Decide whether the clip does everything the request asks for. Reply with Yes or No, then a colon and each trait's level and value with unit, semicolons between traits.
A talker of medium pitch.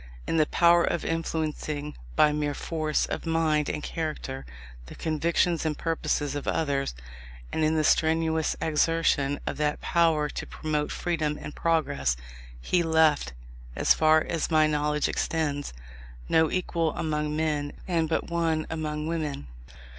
Yes: medium, 155 Hz